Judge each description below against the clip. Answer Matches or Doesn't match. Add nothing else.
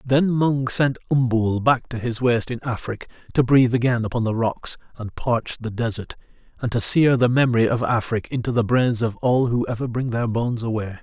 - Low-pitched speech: Matches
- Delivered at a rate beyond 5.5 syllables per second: Doesn't match